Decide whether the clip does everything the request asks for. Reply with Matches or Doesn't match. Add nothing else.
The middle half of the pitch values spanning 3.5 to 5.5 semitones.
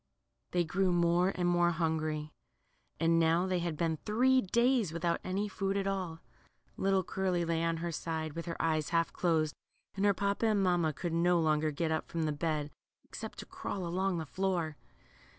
Doesn't match